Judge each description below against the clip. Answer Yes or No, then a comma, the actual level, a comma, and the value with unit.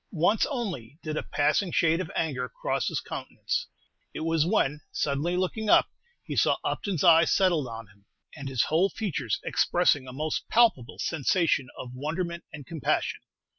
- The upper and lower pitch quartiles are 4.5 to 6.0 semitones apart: Yes, average, 4.8 semitones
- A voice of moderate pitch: Yes, medium, 160 Hz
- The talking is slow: No, average, 165 wpm